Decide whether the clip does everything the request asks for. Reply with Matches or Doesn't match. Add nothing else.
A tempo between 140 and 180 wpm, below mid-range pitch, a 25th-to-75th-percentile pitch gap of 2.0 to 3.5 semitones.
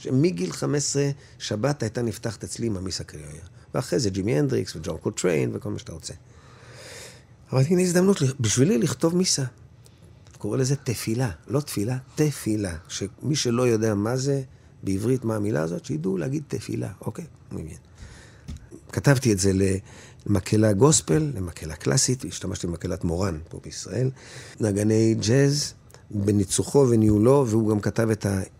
Doesn't match